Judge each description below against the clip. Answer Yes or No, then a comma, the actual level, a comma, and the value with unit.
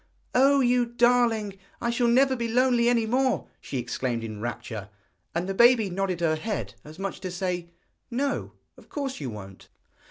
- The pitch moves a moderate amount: No, wide, 6.4 semitones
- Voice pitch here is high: Yes, high, 220 Hz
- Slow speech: No, average, 180 wpm